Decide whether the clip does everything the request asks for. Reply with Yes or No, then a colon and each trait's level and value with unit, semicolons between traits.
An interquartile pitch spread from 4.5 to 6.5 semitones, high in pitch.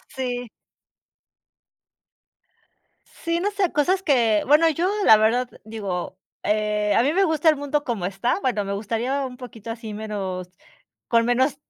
Yes: wide, 5.4 semitones; high, 245 Hz